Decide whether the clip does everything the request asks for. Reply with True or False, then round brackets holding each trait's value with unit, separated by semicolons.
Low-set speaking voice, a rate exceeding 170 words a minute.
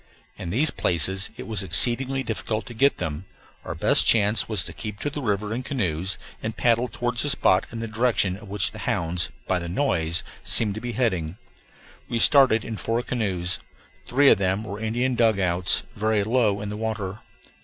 True (110 Hz; 190 wpm)